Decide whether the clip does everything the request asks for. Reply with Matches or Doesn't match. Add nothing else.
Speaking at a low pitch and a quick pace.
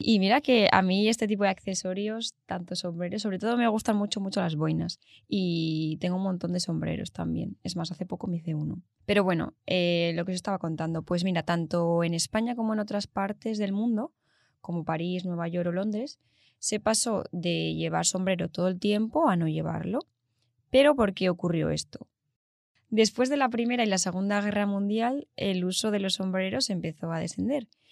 Doesn't match